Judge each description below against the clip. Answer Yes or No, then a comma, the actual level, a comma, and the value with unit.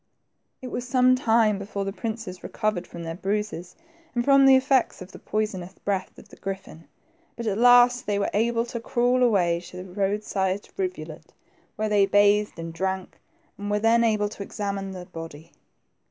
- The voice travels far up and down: No, average, 3.6 semitones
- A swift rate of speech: No, average, 180 wpm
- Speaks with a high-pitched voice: Yes, high, 205 Hz